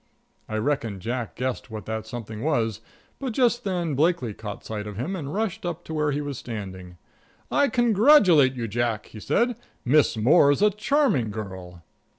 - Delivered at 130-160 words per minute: No, average, 170 wpm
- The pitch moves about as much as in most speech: No, wide, 8.4 semitones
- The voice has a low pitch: Yes, low, 130 Hz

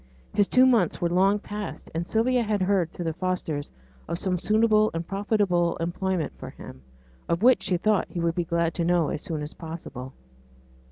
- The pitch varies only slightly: No, average, 3.6 semitones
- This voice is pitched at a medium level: Yes, medium, 180 Hz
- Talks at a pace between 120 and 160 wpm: No, average, 190 wpm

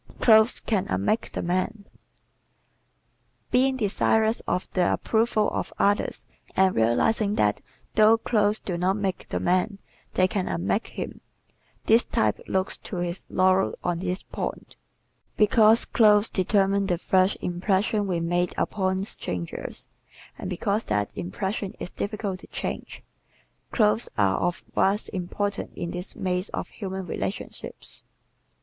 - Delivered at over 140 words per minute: No, slow, 135 wpm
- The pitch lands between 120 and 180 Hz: No, high, 190 Hz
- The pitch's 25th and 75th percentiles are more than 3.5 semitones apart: No, average, 3.0 semitones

